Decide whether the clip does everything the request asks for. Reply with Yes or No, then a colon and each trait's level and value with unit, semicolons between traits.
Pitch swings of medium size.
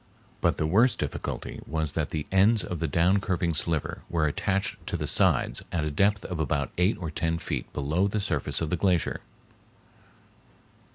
Yes: average, 3.9 semitones